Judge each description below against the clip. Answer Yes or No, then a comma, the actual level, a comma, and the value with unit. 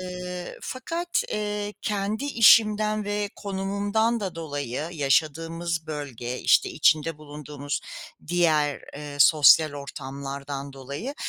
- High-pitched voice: No, medium, 165 Hz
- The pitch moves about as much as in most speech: No, wide, 6.2 semitones